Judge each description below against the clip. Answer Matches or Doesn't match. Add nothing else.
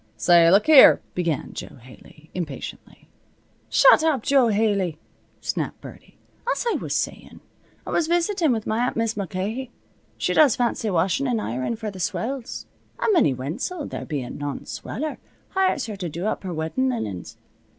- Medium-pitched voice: Doesn't match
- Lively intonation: Matches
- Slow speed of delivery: Doesn't match